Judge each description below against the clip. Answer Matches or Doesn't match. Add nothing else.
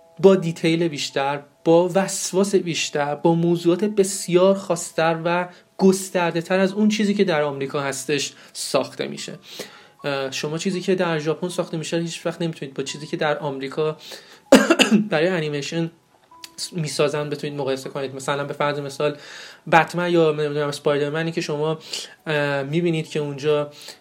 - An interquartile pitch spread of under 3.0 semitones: Doesn't match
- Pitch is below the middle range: Doesn't match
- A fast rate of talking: Doesn't match